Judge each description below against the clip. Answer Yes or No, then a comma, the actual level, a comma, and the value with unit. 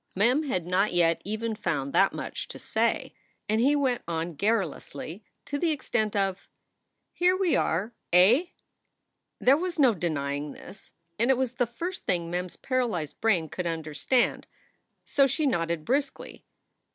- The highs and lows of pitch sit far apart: Yes, wide, 7.5 semitones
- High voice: Yes, high, 210 Hz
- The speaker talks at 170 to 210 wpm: No, average, 160 wpm